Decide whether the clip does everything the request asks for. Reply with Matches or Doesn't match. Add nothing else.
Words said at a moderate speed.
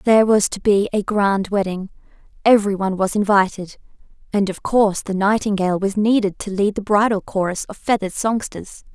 Matches